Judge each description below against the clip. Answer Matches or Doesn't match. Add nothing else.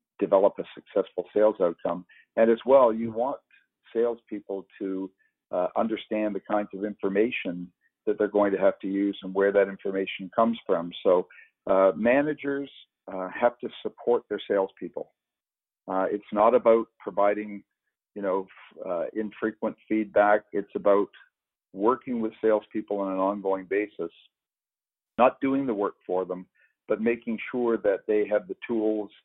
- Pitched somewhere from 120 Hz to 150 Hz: Doesn't match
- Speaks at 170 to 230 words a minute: Doesn't match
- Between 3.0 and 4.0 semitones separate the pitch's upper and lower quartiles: Doesn't match